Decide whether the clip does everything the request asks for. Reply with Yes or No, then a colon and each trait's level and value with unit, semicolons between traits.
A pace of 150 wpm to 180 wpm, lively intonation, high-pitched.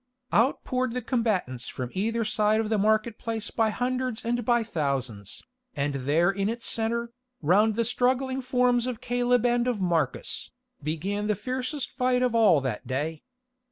Yes: average, 165 wpm; wide, 5.9 semitones; high, 225 Hz